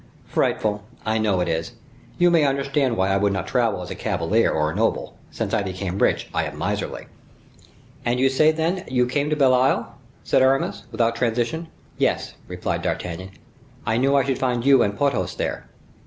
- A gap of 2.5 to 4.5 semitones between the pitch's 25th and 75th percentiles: No, wide, 5.5 semitones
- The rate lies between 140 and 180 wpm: No, average, 190 wpm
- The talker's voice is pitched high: No, low, 120 Hz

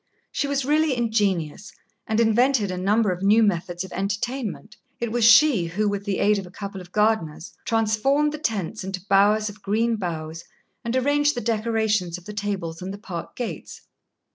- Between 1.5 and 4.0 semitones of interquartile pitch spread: Yes, average, 3.5 semitones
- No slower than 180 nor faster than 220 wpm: Yes, average, 185 wpm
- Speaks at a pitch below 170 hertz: No, high, 210 Hz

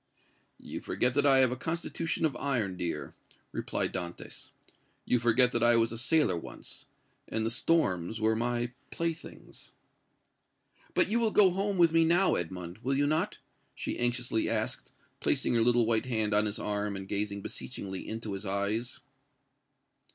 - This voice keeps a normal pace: Yes, average, 165 wpm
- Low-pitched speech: Yes, low, 120 Hz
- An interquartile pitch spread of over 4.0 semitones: Yes, average, 5.3 semitones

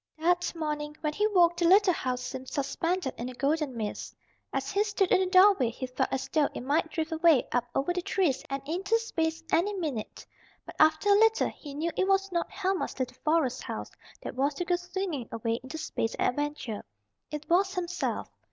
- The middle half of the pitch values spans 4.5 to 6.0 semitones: Yes, average, 5.0 semitones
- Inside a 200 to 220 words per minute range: Yes, fast, 205 wpm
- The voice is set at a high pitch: Yes, very high, 320 Hz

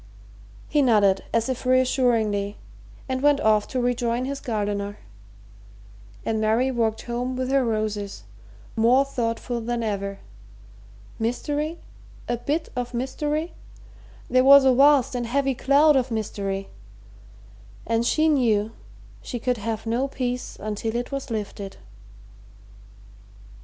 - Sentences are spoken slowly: Yes, slow, 125 wpm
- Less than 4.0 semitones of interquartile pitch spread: Yes, average, 3.4 semitones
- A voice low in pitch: No, high, 240 Hz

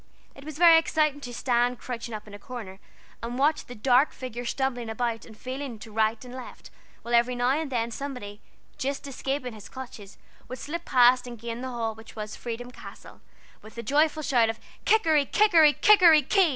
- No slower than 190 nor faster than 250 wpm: Yes, average, 195 wpm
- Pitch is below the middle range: No, very high, 250 Hz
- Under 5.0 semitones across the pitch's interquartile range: Yes, average, 3.6 semitones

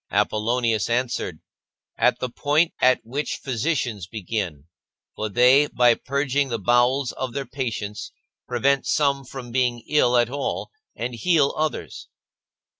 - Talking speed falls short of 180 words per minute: Yes, slow, 135 wpm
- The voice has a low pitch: Yes, low, 125 Hz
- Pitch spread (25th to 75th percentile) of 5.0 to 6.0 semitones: No, average, 3.1 semitones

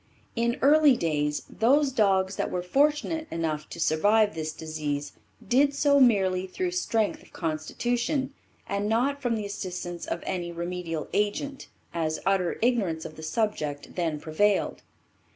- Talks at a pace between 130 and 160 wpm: Yes, average, 145 wpm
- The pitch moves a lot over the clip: Yes, wide, 7.0 semitones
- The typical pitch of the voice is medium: No, high, 195 Hz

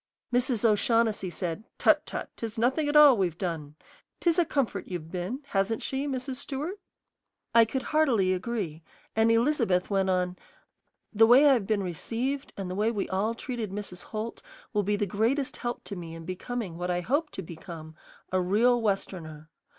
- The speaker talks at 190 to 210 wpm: No, average, 180 wpm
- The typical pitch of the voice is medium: No, high, 215 Hz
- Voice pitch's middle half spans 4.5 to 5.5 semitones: Yes, average, 5.2 semitones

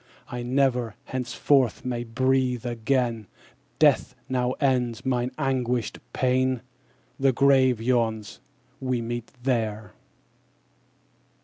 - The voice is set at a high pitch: No, low, 125 Hz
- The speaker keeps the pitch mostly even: Yes, narrow, 1.8 semitones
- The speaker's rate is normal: No, slow, 95 wpm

